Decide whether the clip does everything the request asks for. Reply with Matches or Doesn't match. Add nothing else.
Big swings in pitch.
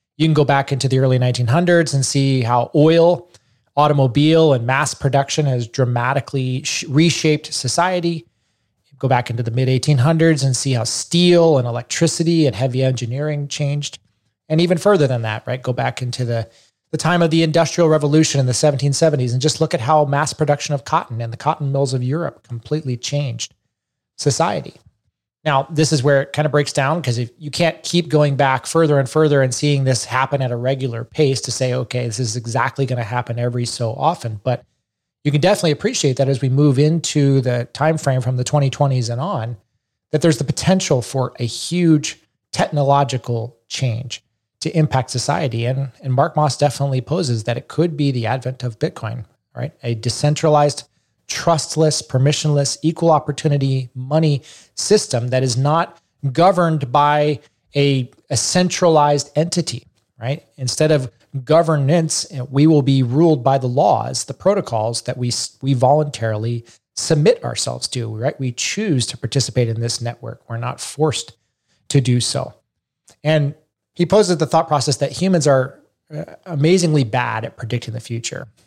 Doesn't match